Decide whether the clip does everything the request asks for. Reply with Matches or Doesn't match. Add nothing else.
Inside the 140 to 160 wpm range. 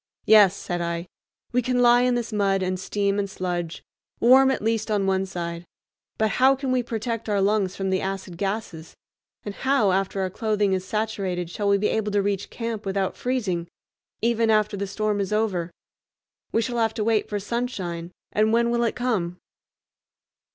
Doesn't match